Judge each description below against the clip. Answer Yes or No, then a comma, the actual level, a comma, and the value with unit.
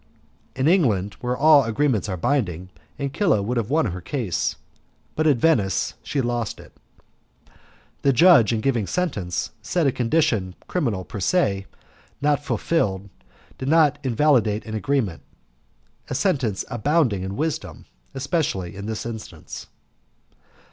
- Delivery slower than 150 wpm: Yes, slow, 135 wpm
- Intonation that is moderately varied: No, wide, 6.3 semitones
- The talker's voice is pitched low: Yes, low, 120 Hz